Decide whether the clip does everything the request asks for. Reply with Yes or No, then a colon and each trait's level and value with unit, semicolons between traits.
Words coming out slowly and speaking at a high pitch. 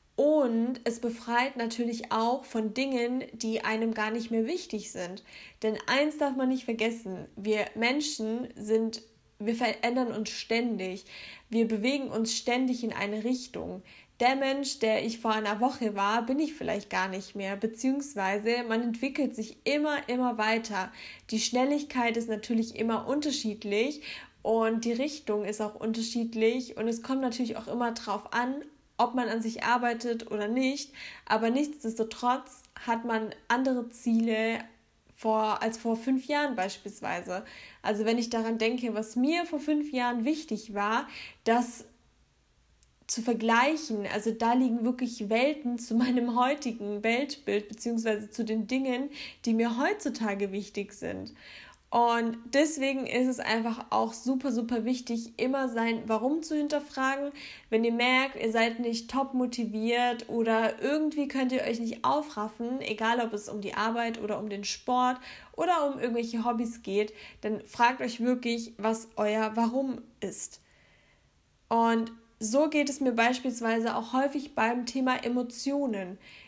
No: average, 150 wpm; high, 235 Hz